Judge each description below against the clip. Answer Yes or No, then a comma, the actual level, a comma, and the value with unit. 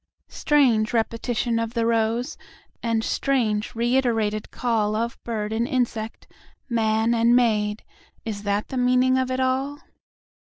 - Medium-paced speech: No, slow, 115 wpm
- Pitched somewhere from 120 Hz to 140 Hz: No, high, 230 Hz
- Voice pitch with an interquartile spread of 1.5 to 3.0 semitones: Yes, narrow, 2.4 semitones